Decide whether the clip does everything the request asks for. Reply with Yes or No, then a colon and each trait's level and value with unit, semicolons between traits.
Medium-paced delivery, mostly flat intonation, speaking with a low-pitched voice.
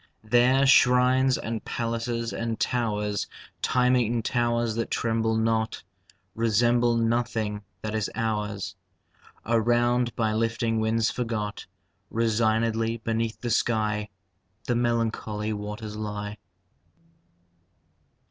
No: slow, 100 wpm; narrow, 1.5 semitones; low, 115 Hz